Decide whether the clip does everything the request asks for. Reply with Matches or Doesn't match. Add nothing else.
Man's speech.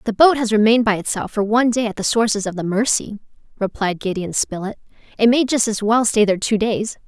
Doesn't match